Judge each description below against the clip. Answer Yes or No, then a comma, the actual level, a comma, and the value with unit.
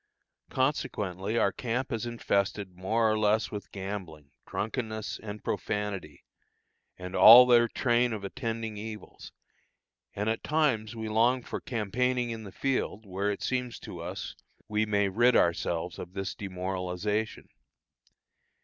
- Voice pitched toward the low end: Yes, low, 110 Hz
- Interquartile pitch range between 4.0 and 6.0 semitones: No, average, 3.2 semitones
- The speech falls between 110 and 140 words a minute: Yes, slow, 135 wpm